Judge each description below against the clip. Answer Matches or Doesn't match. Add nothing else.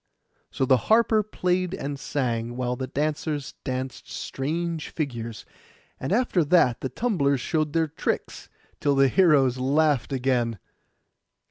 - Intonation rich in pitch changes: Doesn't match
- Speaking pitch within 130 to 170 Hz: Matches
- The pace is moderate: Doesn't match